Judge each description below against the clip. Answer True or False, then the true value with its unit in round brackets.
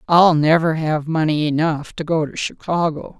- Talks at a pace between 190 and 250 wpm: False (170 wpm)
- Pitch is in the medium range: True (160 Hz)